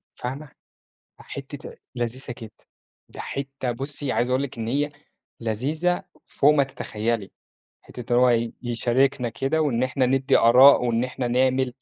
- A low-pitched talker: Yes, low, 125 Hz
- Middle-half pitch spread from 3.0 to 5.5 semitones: No, narrow, 2.5 semitones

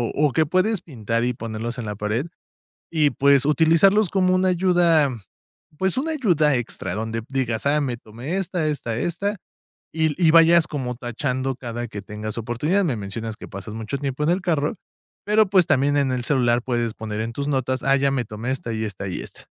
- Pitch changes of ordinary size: No, wide, 6.0 semitones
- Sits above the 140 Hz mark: No, low, 135 Hz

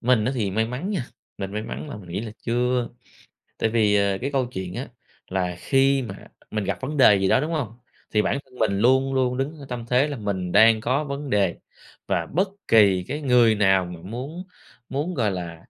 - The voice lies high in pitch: No, low, 115 Hz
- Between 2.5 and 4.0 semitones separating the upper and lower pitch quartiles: No, average, 5.2 semitones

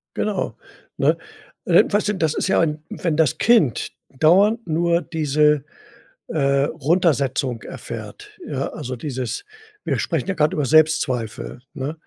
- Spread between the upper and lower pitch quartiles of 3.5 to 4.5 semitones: Yes, average, 3.8 semitones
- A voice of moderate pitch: Yes, medium, 155 Hz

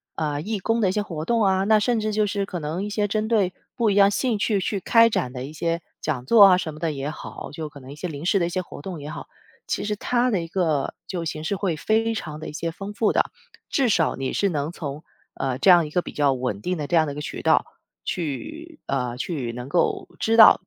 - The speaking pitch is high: No, medium, 175 Hz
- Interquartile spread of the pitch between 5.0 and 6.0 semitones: Yes, wide, 5.6 semitones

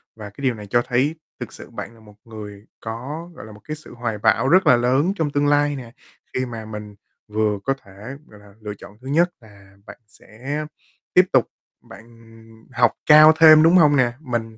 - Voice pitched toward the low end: Yes, low, 120 Hz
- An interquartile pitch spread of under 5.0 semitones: No, average, 5.3 semitones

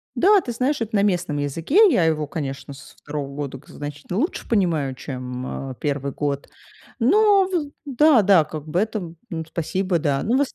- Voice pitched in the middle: Yes, medium, 165 Hz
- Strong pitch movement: Yes, wide, 8.4 semitones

